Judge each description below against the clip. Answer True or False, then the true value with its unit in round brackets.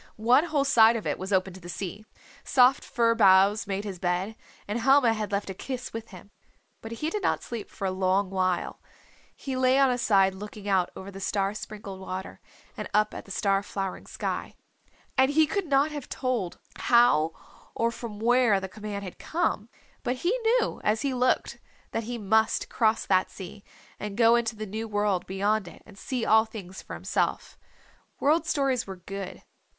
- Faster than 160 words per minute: True (195 wpm)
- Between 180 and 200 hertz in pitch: False (215 Hz)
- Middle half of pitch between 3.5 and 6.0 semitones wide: True (4.0 semitones)